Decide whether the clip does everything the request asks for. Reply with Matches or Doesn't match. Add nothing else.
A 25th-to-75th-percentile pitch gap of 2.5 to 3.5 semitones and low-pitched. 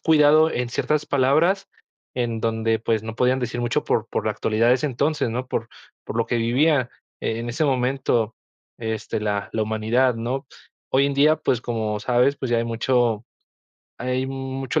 Matches